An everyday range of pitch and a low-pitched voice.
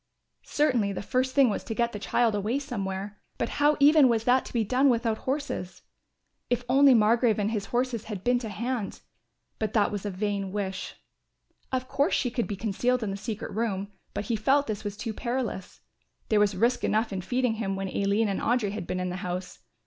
No: average, 3.7 semitones; high, 220 Hz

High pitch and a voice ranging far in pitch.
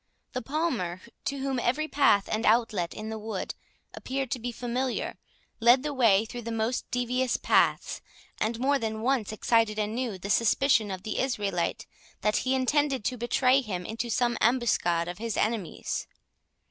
No: high, 235 Hz; average, 3.2 semitones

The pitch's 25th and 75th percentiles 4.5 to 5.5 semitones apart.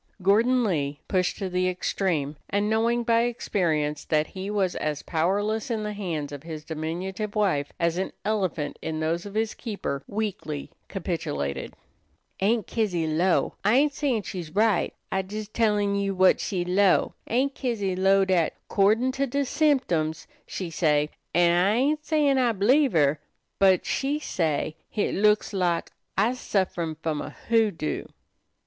Yes: average, 5.0 semitones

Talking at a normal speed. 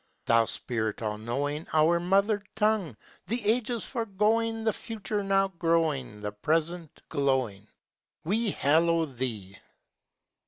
No: slow, 115 wpm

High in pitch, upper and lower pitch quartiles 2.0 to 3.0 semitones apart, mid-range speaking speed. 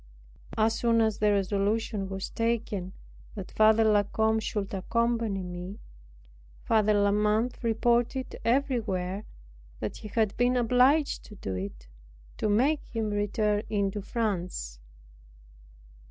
No: high, 215 Hz; narrow, 2.6 semitones; slow, 125 wpm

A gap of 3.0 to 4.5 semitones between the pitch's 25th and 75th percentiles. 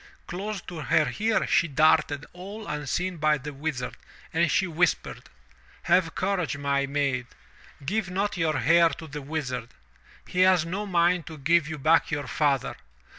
Yes: average, 3.7 semitones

